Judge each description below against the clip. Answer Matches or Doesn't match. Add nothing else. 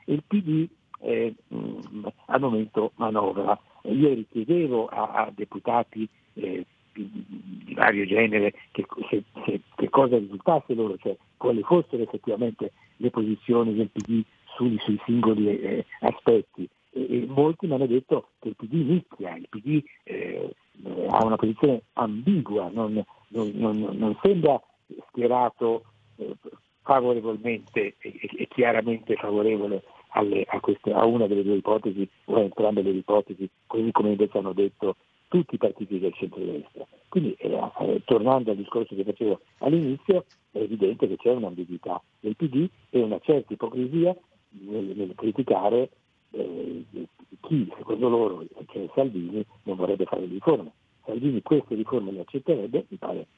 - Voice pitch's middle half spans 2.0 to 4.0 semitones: Matches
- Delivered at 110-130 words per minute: Doesn't match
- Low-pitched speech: Matches